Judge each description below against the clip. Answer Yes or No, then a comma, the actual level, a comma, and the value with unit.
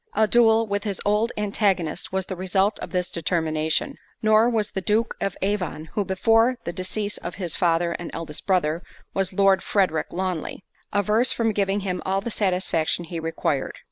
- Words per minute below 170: No, average, 175 wpm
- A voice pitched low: No, high, 190 Hz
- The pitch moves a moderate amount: Yes, average, 3.3 semitones